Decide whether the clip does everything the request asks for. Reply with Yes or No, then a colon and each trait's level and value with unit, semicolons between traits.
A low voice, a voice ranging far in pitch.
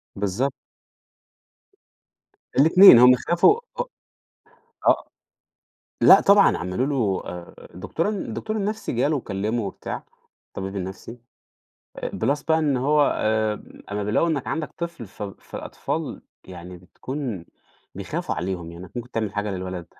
Yes: low, 115 Hz; wide, 7.5 semitones